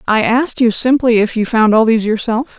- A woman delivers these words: Yes, female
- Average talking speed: No, fast, 230 wpm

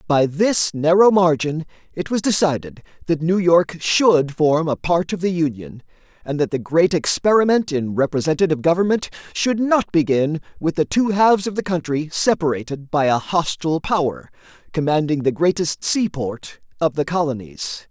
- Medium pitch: Yes, medium, 165 Hz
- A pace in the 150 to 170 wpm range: Yes, average, 160 wpm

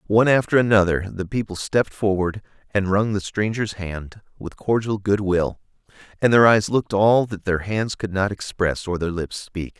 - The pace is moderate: Yes, average, 190 wpm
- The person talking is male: Yes, male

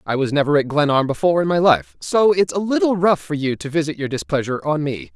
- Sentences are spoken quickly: Yes, fast, 255 wpm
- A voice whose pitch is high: No, medium, 150 Hz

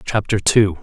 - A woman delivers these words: No, male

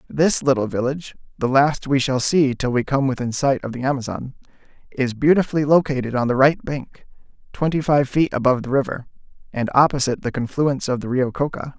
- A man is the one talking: Yes, male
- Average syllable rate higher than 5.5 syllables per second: Yes, 5.9 syllables/s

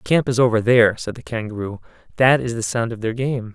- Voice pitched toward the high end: No, low, 115 Hz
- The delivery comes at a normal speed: No, fast, 255 wpm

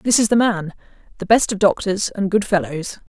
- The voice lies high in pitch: Yes, high, 200 Hz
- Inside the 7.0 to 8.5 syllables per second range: No, 5.1 syllables/s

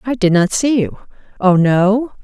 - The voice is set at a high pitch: Yes, high, 205 Hz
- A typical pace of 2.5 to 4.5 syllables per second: Yes, 4.4 syllables/s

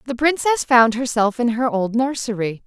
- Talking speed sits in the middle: Yes, average, 180 wpm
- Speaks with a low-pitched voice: No, high, 240 Hz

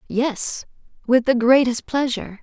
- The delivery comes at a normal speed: No, slow, 125 wpm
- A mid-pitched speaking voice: No, high, 245 Hz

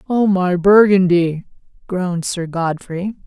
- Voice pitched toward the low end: No, medium, 185 Hz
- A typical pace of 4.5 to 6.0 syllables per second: No, 3.9 syllables/s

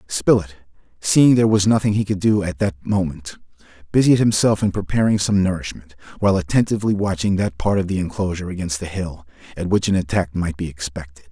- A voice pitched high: No, very low, 95 Hz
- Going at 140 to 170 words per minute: No, average, 185 wpm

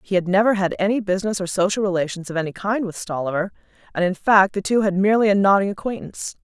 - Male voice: No, female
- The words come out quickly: Yes, fast, 225 wpm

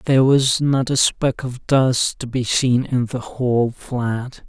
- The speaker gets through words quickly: No, average, 190 wpm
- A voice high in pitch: No, low, 125 Hz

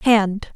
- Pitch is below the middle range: No, high, 210 Hz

